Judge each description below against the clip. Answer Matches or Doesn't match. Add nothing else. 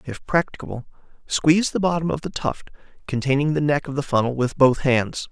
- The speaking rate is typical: Matches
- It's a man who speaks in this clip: Matches